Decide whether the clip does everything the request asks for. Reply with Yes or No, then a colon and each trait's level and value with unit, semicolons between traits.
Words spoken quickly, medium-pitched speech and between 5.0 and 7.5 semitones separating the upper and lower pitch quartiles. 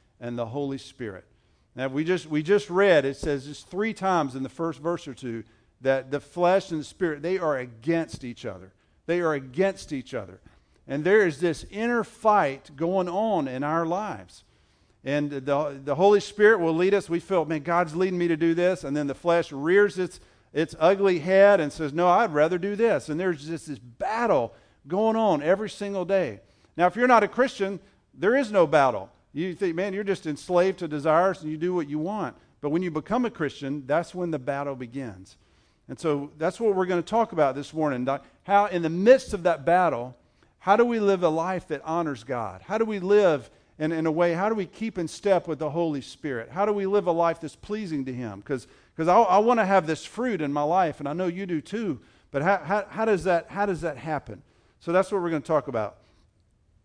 Yes: fast, 230 wpm; medium, 165 Hz; wide, 5.6 semitones